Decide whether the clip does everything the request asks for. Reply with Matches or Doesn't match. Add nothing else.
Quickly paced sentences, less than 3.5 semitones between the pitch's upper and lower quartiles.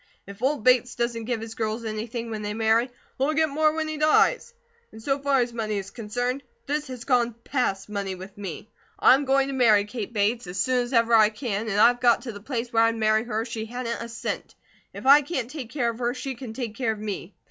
Matches